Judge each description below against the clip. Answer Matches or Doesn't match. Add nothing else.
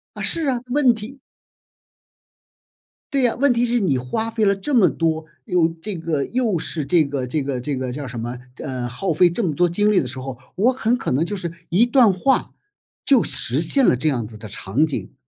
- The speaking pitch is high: Doesn't match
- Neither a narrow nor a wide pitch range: Doesn't match